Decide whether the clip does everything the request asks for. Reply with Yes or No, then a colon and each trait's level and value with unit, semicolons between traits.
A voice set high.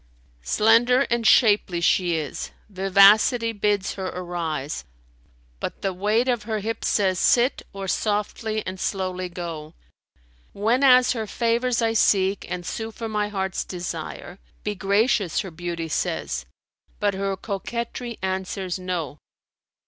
Yes: high, 195 Hz